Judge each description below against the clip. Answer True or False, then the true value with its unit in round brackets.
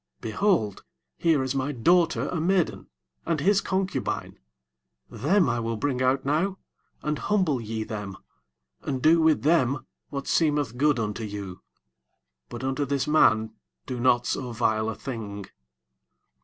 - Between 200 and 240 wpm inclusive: False (145 wpm)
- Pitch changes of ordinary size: False (5.8 semitones)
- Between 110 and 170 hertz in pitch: True (135 Hz)